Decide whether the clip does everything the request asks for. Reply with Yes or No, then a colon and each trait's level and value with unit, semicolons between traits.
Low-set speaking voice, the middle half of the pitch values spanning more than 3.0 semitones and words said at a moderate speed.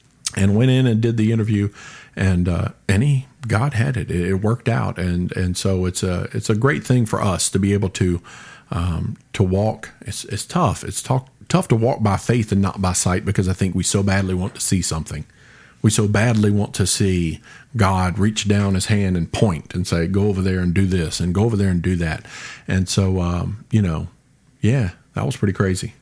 No: low, 100 Hz; average, 3.6 semitones; fast, 220 wpm